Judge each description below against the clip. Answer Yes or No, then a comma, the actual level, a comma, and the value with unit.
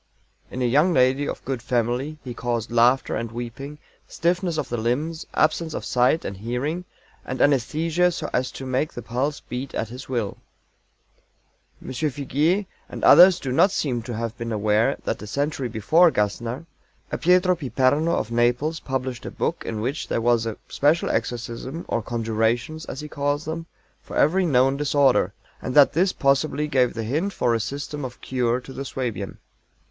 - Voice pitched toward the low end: Yes, low, 130 Hz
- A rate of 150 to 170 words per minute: No, average, 180 wpm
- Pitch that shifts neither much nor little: Yes, average, 4.3 semitones